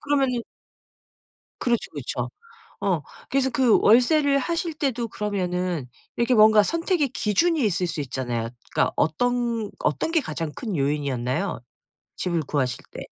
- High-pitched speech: Yes, high, 215 Hz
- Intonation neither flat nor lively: No, wide, 8.9 semitones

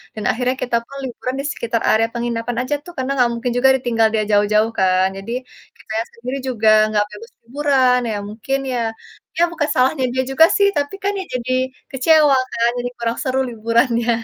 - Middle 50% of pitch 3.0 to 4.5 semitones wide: No, narrow, 2.6 semitones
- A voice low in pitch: No, high, 245 Hz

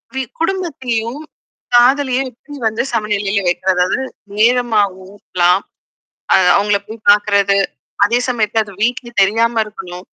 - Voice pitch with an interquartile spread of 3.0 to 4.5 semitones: Yes, average, 3.4 semitones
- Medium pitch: No, high, 220 Hz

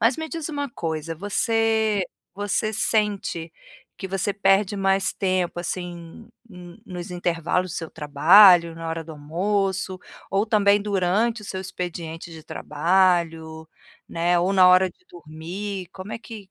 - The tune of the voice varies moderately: Yes, average, 3.4 semitones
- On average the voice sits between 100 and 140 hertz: No, medium, 185 Hz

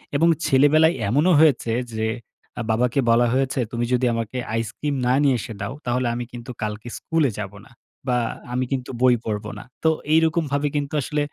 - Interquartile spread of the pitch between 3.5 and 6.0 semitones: Yes, average, 3.8 semitones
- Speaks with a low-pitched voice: Yes, low, 130 Hz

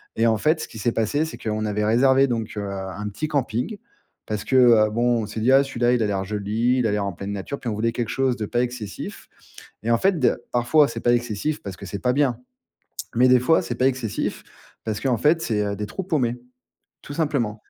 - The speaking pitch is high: No, low, 120 Hz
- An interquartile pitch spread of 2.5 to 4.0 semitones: Yes, average, 3.5 semitones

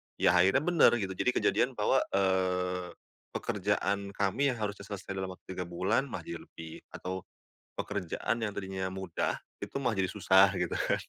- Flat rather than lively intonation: Yes, narrow, 2.0 semitones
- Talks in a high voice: No, very low, 95 Hz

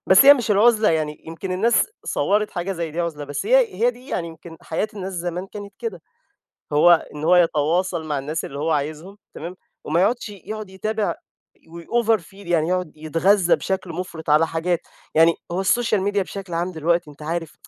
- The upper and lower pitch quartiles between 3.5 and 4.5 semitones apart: Yes, average, 3.9 semitones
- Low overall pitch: No, medium, 175 Hz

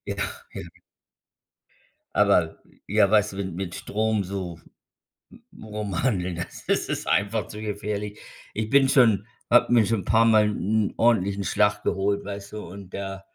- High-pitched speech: No, low, 105 Hz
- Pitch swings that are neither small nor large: No, narrow, 1.9 semitones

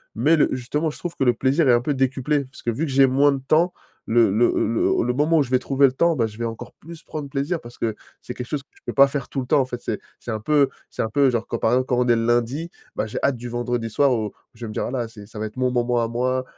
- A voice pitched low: Yes, low, 125 Hz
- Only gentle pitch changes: No, average, 3.1 semitones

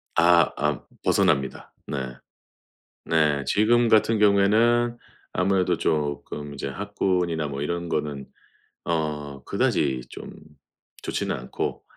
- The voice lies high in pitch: No, very low, 80 Hz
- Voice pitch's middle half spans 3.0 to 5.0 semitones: No, wide, 5.4 semitones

